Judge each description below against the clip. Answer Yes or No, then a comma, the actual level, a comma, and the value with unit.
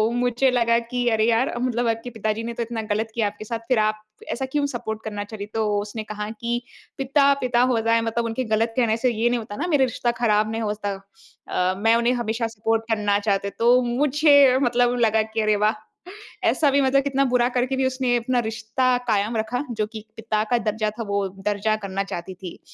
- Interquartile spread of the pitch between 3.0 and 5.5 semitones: No, narrow, 2.5 semitones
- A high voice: Yes, high, 230 Hz